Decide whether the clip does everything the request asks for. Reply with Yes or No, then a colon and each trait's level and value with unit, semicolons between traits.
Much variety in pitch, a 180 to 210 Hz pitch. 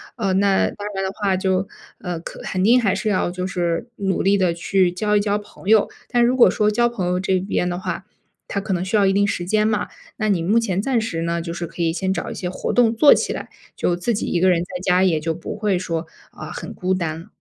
No: average, 2.8 semitones; high, 190 Hz